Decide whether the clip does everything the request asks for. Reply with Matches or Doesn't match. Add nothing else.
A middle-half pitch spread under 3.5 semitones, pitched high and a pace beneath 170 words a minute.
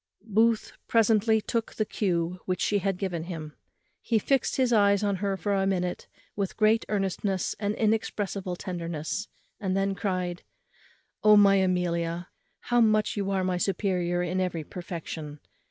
Matches